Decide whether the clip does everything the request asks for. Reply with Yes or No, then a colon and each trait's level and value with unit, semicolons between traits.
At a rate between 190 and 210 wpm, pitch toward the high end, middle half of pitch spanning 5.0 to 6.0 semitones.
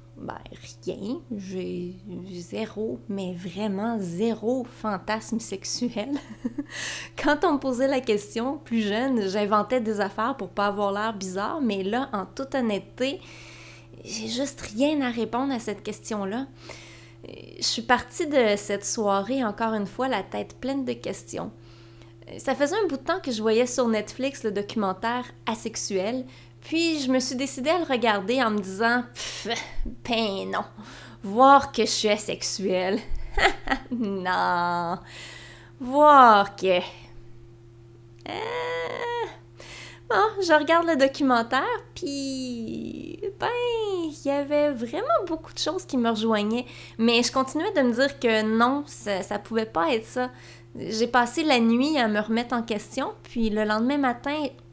No: average, 145 wpm; high, 230 Hz; average, 5.3 semitones